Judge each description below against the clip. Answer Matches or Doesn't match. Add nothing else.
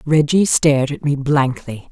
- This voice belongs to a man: Doesn't match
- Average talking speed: Matches